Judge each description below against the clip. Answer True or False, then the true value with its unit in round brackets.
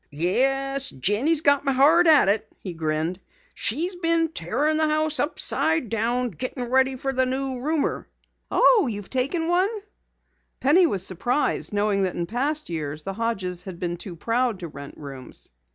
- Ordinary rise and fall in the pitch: False (7.9 semitones)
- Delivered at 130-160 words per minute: False (170 wpm)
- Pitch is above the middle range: True (250 Hz)